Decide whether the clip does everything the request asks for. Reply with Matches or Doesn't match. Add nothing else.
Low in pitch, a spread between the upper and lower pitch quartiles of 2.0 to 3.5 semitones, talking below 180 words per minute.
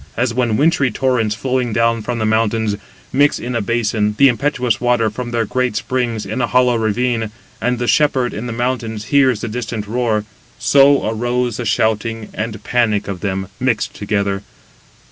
Matches